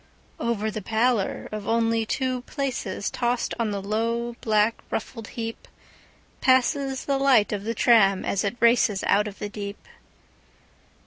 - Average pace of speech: No, slow, 130 wpm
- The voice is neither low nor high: No, high, 225 Hz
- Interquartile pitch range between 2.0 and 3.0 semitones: Yes, narrow, 2.5 semitones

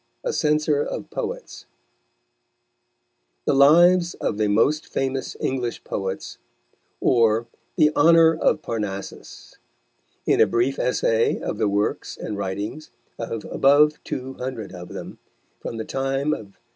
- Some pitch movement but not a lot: No, wide, 5.8 semitones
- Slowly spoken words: Yes, slow, 130 wpm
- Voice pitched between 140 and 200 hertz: No, low, 130 Hz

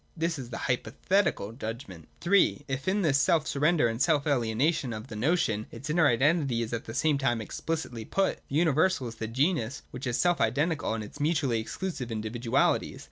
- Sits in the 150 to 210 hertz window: No, low, 135 Hz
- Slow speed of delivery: No, average, 185 wpm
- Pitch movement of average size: No, wide, 5.7 semitones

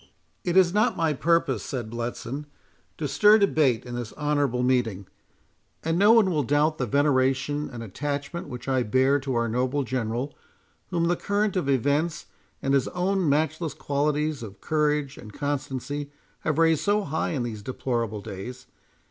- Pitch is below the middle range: No, medium, 145 Hz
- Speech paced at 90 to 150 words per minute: No, average, 165 wpm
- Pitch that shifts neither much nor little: Yes, average, 4.2 semitones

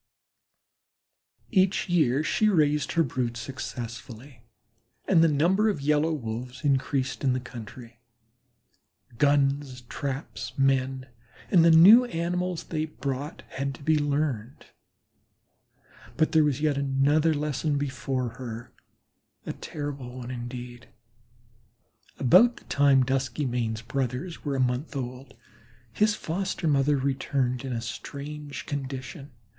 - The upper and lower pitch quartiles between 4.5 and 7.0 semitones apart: No, average, 3.3 semitones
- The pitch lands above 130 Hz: Yes, medium, 140 Hz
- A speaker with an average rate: No, slow, 120 wpm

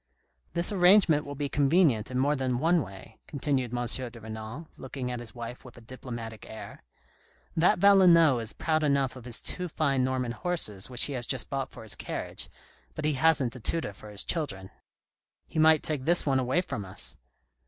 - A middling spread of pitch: Yes, average, 4.9 semitones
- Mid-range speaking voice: No, low, 130 Hz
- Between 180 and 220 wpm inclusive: Yes, average, 200 wpm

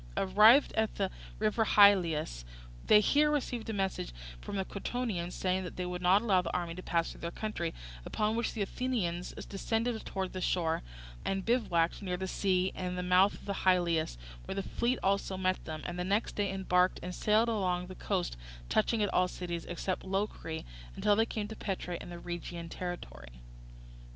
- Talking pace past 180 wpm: Yes, average, 190 wpm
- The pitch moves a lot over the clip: No, average, 3.1 semitones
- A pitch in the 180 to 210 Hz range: Yes, high, 190 Hz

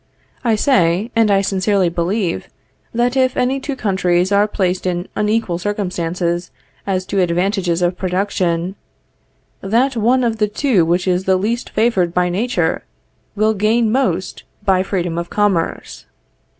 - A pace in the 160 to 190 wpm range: No, average, 145 wpm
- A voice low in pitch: No, high, 195 Hz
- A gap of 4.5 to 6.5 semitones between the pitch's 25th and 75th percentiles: No, average, 3.7 semitones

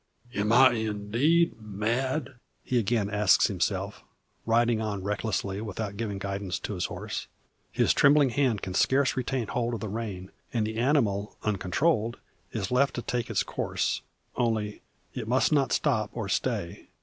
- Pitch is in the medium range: No, low, 110 Hz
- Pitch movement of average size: Yes, average, 3.5 semitones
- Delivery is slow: No, average, 155 wpm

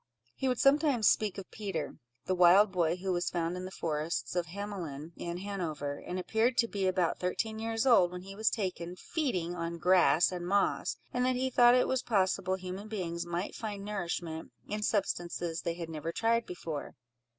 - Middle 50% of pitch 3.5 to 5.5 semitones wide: Yes, average, 3.9 semitones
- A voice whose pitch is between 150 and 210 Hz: Yes, medium, 185 Hz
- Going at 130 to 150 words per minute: No, average, 190 wpm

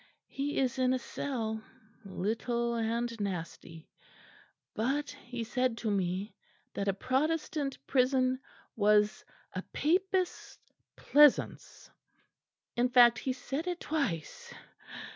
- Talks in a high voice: Yes, high, 245 Hz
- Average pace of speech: No, slow, 105 wpm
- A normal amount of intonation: Yes, average, 4.1 semitones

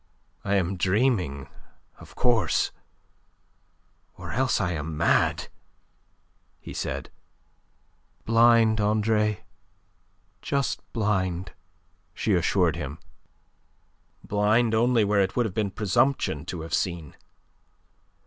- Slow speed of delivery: Yes, slow, 100 wpm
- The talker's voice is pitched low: Yes, low, 105 Hz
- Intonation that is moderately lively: Yes, average, 4.3 semitones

